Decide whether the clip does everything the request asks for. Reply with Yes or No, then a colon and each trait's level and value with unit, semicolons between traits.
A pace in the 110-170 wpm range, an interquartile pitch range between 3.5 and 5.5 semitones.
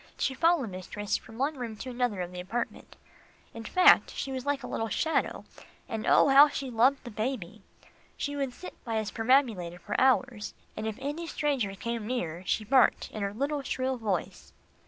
No: average, 190 wpm; average, 4.1 semitones